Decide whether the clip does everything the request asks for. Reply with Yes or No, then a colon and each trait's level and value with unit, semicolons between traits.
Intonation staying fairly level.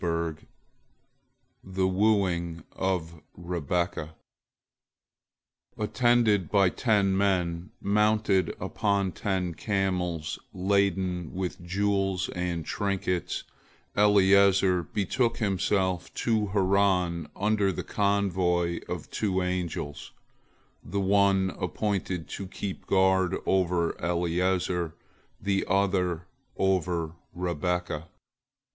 Yes: narrow, 2.2 semitones